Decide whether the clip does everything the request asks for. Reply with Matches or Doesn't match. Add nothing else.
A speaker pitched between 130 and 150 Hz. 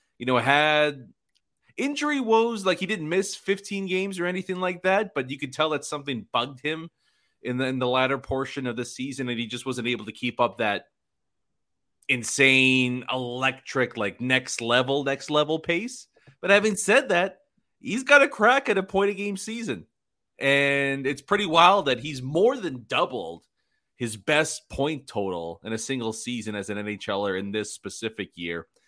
Matches